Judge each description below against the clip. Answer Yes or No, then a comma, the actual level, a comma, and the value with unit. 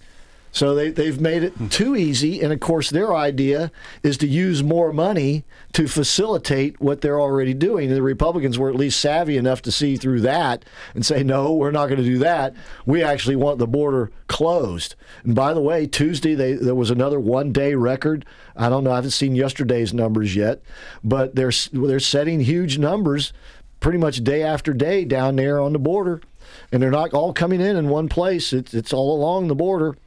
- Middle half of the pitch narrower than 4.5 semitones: Yes, average, 2.9 semitones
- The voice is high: No, medium, 140 Hz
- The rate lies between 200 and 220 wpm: Yes, fast, 205 wpm